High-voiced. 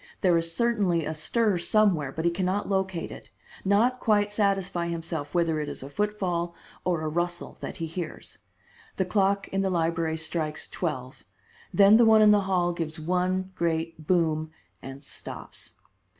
No: medium, 175 Hz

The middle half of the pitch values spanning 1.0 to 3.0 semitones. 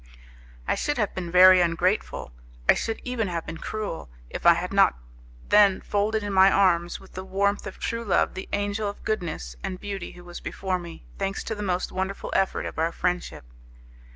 Yes: narrow, 2.5 semitones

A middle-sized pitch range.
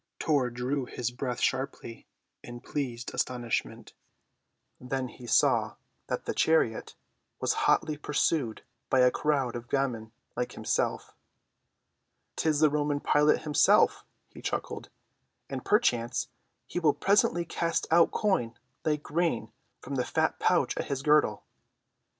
Yes: average, 3.7 semitones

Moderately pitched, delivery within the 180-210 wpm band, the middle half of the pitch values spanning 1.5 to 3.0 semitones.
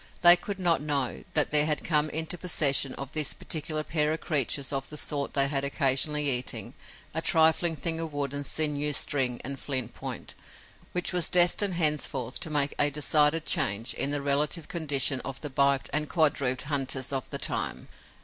Yes: medium, 145 Hz; average, 185 wpm; narrow, 2.4 semitones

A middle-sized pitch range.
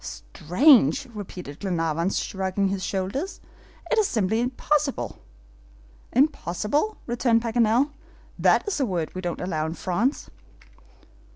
No: wide, 6.8 semitones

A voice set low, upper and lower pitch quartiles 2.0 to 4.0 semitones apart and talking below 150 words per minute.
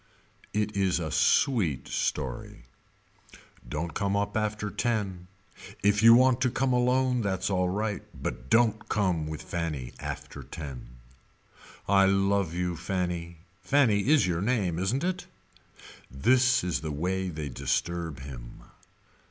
No: very low, 95 Hz; average, 5.0 semitones; slow, 135 wpm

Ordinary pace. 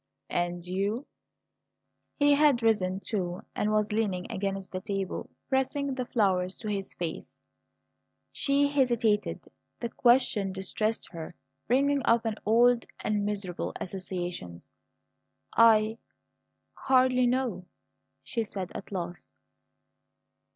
No: slow, 110 wpm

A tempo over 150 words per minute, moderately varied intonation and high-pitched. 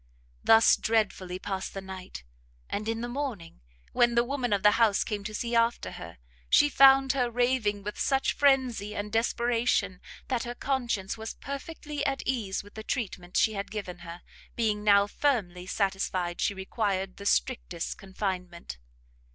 Yes: average, 160 wpm; average, 4.1 semitones; high, 215 Hz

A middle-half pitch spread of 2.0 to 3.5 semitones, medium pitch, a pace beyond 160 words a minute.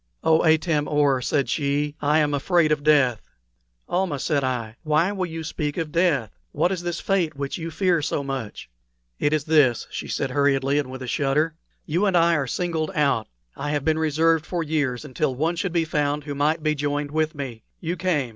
Yes: average, 2.7 semitones; medium, 150 Hz; fast, 205 wpm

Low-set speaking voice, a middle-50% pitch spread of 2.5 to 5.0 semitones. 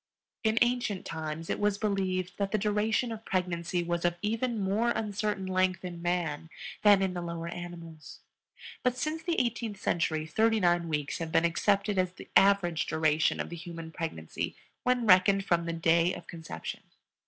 No: medium, 185 Hz; average, 3.7 semitones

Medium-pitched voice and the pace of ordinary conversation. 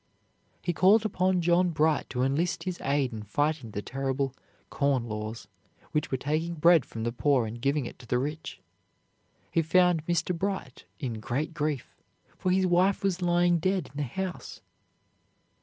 Yes: medium, 155 Hz; average, 170 wpm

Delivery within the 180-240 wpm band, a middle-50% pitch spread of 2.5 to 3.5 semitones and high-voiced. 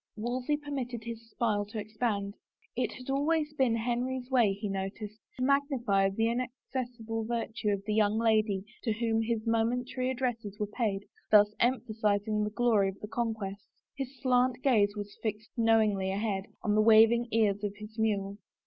No: average, 165 wpm; average, 2.9 semitones; high, 225 Hz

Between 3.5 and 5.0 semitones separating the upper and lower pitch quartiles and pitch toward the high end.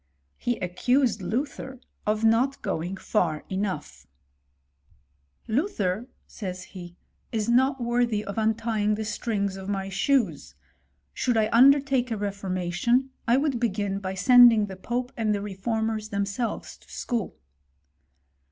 Yes: average, 4.0 semitones; high, 215 Hz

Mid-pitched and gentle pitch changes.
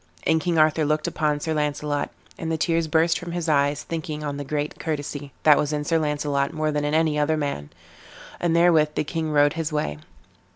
Yes: medium, 150 Hz; narrow, 1.7 semitones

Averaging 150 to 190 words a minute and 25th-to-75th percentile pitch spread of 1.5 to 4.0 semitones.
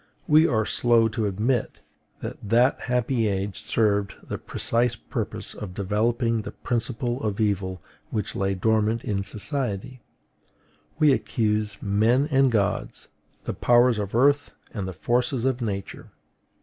No: slow, 135 wpm; average, 3.2 semitones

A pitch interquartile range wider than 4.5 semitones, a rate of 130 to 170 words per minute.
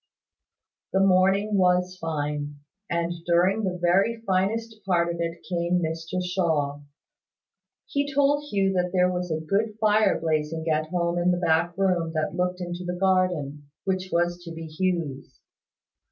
No: narrow, 2.6 semitones; average, 155 wpm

